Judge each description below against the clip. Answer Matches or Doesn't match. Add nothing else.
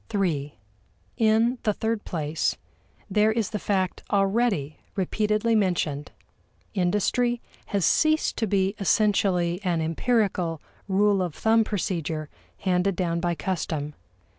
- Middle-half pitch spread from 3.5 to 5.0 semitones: Matches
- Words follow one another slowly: Matches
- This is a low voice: Doesn't match